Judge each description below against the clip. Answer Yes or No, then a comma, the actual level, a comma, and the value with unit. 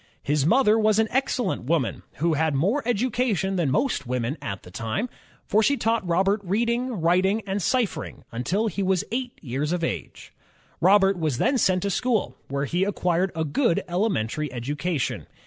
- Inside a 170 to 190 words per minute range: Yes, average, 175 wpm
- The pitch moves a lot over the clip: Yes, wide, 6.6 semitones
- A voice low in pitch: No, medium, 185 Hz